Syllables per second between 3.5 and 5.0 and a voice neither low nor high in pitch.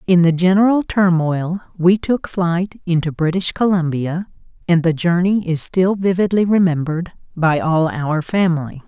Yes: 4.6 syllables/s; medium, 175 Hz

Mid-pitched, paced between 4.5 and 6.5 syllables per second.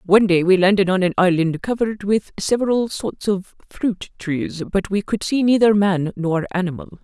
No: high, 195 Hz; 5.0 syllables/s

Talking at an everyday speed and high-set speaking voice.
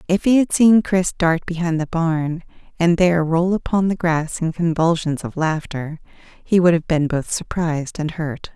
No: average, 190 wpm; medium, 165 Hz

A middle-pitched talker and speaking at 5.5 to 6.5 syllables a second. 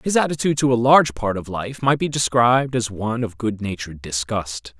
No: low, 120 Hz; 5.8 syllables/s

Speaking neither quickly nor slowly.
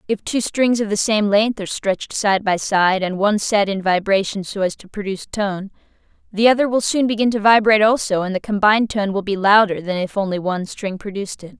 No: fast, 230 wpm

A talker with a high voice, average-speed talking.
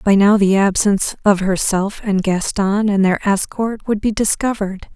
Yes: high, 200 Hz; average, 170 wpm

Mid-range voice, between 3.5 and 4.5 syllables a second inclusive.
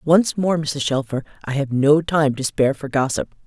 No: medium, 145 Hz; 5.0 syllables/s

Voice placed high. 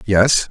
No: low, 105 Hz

